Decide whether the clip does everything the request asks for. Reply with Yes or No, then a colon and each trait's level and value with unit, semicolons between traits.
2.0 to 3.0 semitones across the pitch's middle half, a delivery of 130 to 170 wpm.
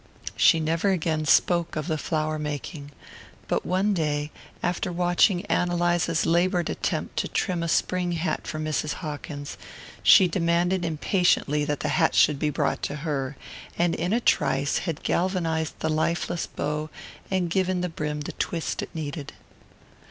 Yes: average, 2.7 semitones; average, 160 wpm